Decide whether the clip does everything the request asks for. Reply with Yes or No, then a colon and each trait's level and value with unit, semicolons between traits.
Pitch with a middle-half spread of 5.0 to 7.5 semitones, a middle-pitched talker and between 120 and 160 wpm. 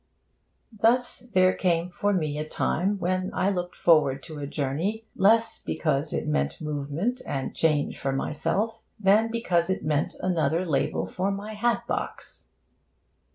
Yes: average, 5.3 semitones; medium, 180 Hz; average, 150 wpm